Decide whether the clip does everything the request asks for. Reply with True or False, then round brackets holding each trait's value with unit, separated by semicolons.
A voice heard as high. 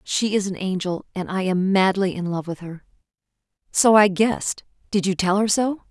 True (195 Hz)